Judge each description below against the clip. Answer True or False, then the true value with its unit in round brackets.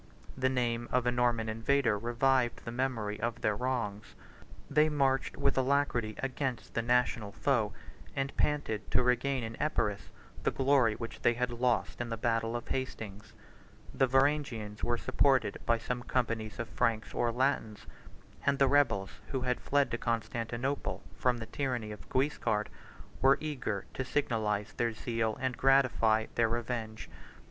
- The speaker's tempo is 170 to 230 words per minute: False (155 wpm)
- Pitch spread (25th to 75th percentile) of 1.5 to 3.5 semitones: True (3.0 semitones)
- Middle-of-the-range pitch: False (120 Hz)